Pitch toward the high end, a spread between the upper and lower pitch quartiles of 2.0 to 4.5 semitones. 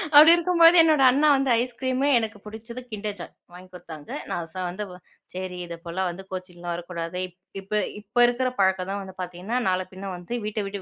No: high, 195 Hz; average, 5.2 semitones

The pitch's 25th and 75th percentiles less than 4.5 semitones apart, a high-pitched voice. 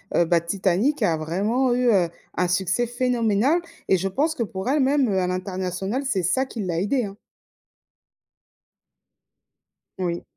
No: wide, 5.5 semitones; high, 200 Hz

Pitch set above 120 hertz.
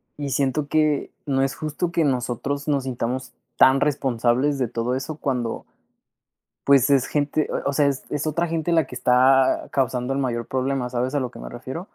Yes: low, 135 Hz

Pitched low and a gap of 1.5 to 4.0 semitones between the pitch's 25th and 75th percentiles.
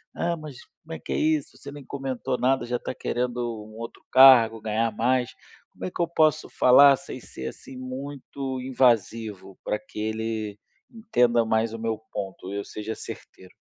Yes: low, 120 Hz; average, 3.5 semitones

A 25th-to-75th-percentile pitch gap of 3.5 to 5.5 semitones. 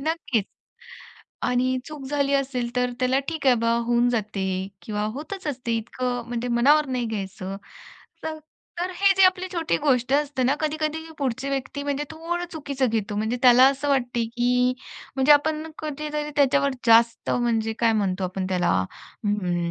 Yes: average, 4.3 semitones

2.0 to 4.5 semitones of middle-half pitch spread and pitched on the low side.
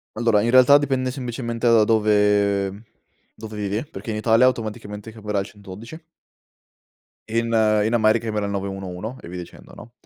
Yes: narrow, 2.3 semitones; low, 110 Hz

